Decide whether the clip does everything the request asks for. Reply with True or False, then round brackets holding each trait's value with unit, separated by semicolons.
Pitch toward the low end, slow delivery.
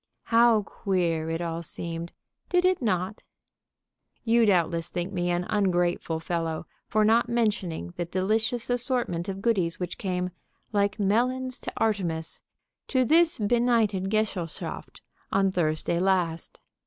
False (195 Hz; 130 wpm)